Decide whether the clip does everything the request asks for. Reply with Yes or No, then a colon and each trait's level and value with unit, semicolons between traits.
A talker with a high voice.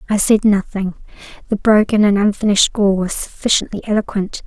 Yes: high, 205 Hz